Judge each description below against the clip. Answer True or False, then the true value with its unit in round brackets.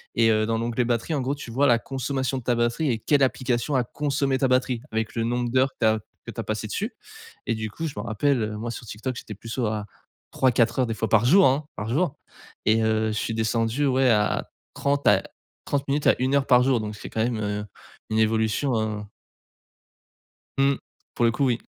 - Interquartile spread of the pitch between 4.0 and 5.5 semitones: False (3.3 semitones)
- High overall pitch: False (120 Hz)